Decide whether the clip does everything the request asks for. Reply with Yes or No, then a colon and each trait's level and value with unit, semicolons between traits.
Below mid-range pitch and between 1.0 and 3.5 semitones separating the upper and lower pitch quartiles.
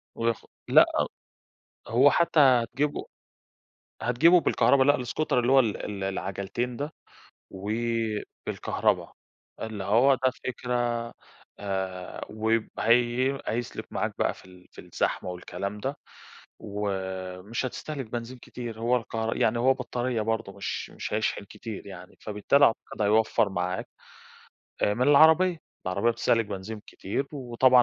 No: low, 115 Hz; average, 4.2 semitones